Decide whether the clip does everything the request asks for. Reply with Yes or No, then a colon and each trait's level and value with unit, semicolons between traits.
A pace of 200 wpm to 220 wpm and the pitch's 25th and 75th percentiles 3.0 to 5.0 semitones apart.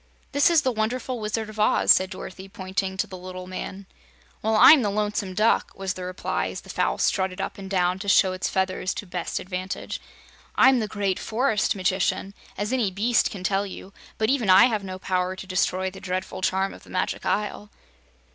No: fast, 205 wpm; narrow, 2.4 semitones